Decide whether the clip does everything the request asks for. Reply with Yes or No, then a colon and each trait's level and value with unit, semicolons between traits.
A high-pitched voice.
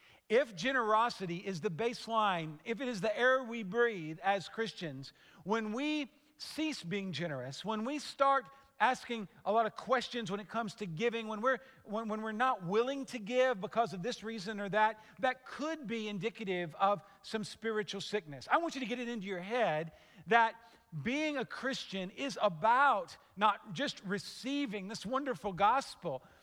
Yes: high, 220 Hz